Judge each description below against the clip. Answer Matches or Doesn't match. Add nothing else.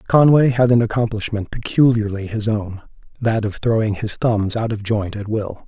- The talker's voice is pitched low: Matches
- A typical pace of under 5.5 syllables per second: Matches